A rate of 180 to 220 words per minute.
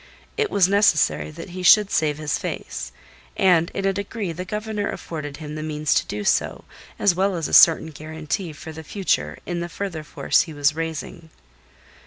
Yes: average, 190 wpm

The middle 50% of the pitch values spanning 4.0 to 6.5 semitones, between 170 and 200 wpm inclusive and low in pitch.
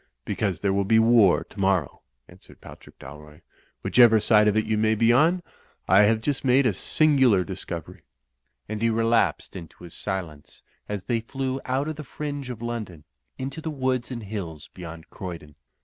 Yes: wide, 5.4 semitones; average, 175 wpm; low, 110 Hz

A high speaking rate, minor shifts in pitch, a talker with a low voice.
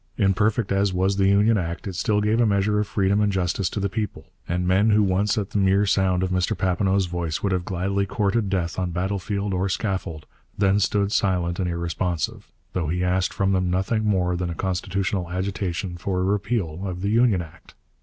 Yes: fast, 210 wpm; narrow, 2.0 semitones; very low, 95 Hz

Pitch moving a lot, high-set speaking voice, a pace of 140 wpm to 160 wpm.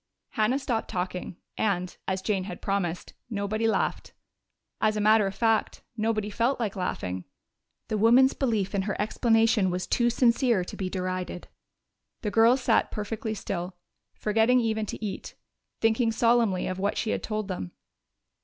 No: average, 3.1 semitones; high, 215 Hz; average, 155 wpm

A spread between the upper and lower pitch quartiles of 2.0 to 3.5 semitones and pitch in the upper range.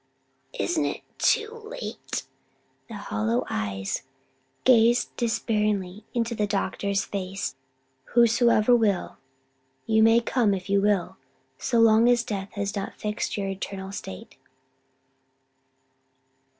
Yes: average, 3.1 semitones; high, 210 Hz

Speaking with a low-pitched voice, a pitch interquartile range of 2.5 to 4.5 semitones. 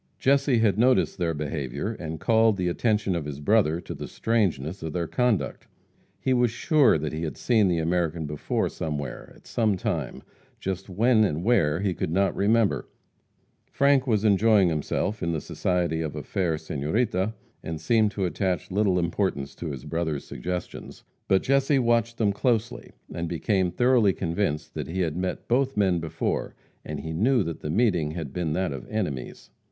No: very low, 95 Hz; wide, 5.5 semitones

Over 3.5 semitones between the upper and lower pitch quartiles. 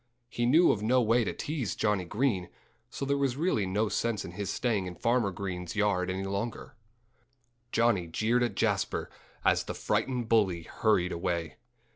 Yes: average, 4.4 semitones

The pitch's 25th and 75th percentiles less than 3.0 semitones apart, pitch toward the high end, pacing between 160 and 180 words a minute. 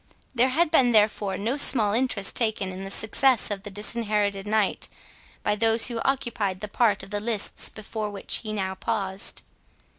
Yes: narrow, 2.6 semitones; high, 215 Hz; average, 175 wpm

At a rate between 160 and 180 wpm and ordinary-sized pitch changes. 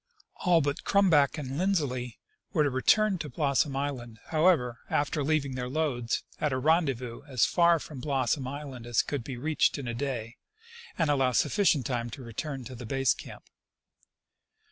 Yes: average, 170 wpm; average, 3.7 semitones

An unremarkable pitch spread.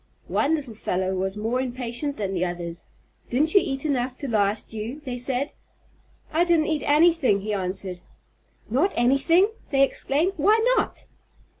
No: wide, 6.4 semitones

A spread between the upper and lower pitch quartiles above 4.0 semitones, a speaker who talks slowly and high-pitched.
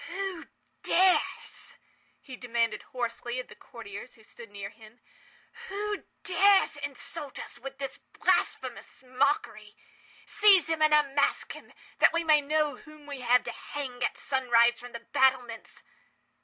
Yes: average, 4.5 semitones; slow, 130 wpm; very high, 270 Hz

